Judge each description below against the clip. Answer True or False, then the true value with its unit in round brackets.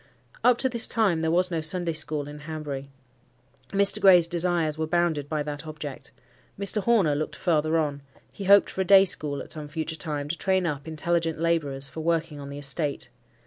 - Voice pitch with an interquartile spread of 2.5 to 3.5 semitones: True (2.9 semitones)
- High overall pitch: False (160 Hz)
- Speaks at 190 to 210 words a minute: True (195 wpm)